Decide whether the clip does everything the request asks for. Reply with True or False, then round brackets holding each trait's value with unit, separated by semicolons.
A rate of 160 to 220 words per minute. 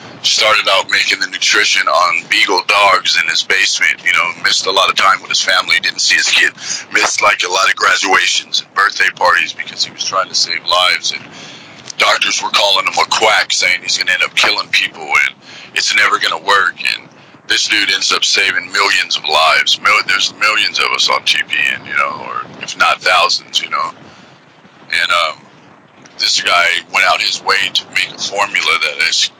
True (200 wpm)